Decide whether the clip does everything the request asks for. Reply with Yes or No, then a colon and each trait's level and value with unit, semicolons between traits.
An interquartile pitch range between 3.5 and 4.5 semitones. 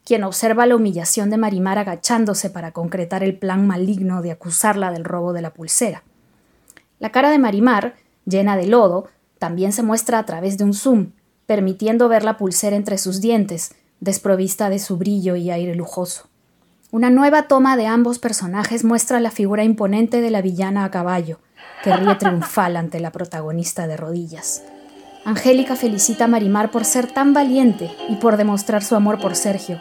Yes: average, 3.9 semitones